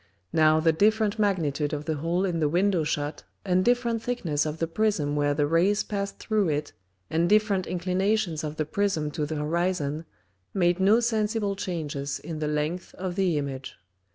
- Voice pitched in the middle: Yes, medium, 170 Hz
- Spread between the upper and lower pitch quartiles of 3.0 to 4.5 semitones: No, average, 4.9 semitones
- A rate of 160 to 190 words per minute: Yes, average, 180 wpm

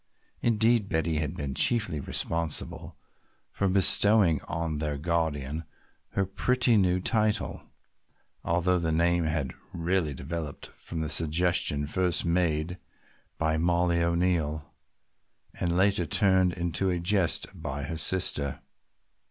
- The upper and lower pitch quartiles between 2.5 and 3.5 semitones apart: Yes, average, 2.9 semitones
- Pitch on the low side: Yes, very low, 85 Hz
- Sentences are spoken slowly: Yes, slow, 120 wpm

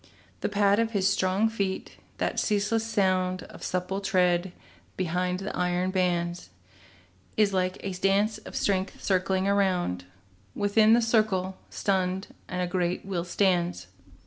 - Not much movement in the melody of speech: Yes, narrow, 1.8 semitones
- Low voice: No, high, 190 Hz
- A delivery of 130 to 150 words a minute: Yes, average, 140 wpm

